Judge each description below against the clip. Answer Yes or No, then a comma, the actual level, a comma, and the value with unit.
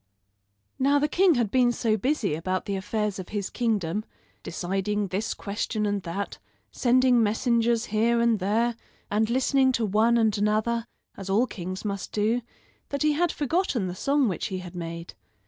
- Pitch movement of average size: Yes, average, 3.5 semitones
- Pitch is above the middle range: Yes, high, 215 Hz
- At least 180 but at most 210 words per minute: No, average, 170 wpm